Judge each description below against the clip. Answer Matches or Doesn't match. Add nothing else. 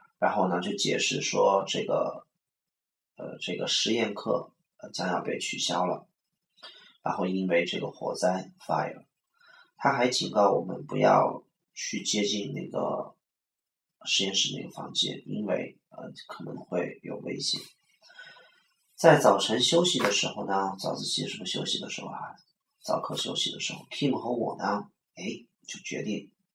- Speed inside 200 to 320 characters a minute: Matches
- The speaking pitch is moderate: Doesn't match